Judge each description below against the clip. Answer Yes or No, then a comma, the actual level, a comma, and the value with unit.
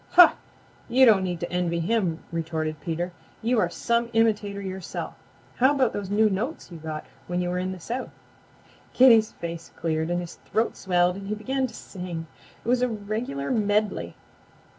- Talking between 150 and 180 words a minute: Yes, average, 175 wpm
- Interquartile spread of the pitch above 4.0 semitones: Yes, average, 4.7 semitones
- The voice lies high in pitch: Yes, high, 195 Hz